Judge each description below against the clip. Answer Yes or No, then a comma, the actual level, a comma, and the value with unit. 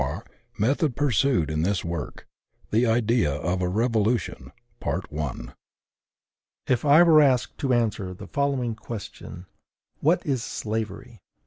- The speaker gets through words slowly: Yes, slow, 125 wpm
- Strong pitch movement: Yes, wide, 6.3 semitones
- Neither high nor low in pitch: No, low, 115 Hz